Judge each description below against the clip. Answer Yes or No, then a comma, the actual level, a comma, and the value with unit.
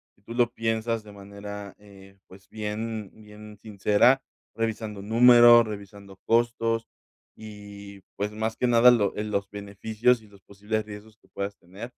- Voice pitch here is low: Yes, low, 105 Hz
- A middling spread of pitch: No, narrow, 2.0 semitones